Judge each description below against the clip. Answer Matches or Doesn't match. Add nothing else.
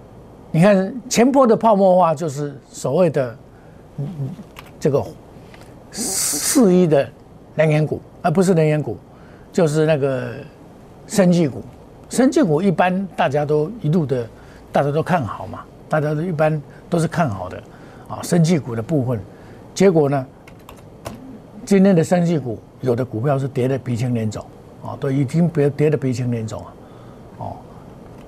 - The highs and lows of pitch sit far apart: Matches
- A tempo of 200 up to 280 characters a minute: Matches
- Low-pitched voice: Doesn't match